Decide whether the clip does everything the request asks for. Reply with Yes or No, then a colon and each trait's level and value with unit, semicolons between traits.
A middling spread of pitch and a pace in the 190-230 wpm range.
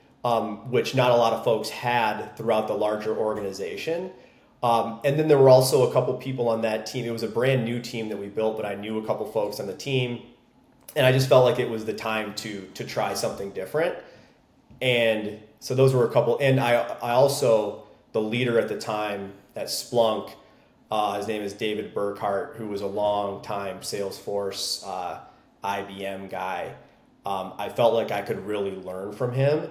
Yes: average, 3.5 semitones; average, 200 wpm